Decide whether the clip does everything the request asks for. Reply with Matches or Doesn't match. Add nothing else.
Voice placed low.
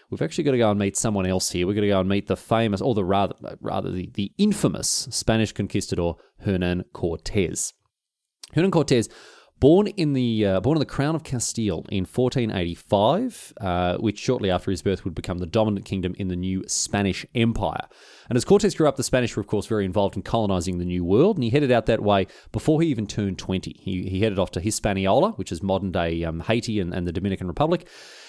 Matches